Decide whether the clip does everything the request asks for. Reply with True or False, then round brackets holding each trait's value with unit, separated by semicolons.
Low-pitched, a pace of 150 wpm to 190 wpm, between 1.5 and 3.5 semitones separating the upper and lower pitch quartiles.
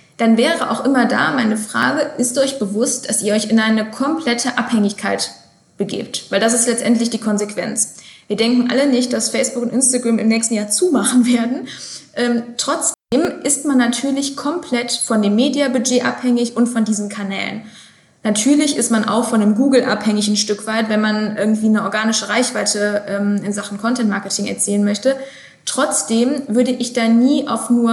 False (230 Hz; 175 wpm; 2.8 semitones)